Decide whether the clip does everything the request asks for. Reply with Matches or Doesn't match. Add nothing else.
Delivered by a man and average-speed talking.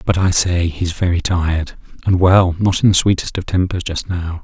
Matches